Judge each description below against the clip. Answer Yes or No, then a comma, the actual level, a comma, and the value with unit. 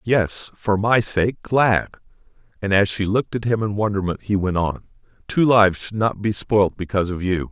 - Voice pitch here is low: Yes, low, 100 Hz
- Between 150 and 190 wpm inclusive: No, average, 200 wpm